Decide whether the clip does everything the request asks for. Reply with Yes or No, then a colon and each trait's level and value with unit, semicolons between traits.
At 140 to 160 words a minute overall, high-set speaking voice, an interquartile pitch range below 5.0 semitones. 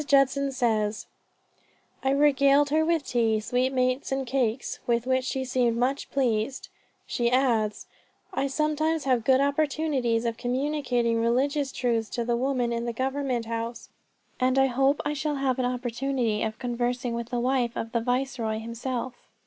Yes: average, 155 wpm; very high, 255 Hz; narrow, 2.6 semitones